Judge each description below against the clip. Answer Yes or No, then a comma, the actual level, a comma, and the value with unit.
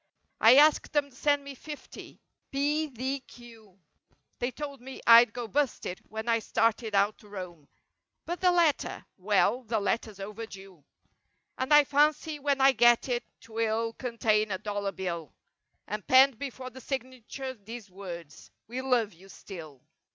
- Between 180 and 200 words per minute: No, average, 150 wpm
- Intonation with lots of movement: No, average, 4.7 semitones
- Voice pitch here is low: No, high, 230 Hz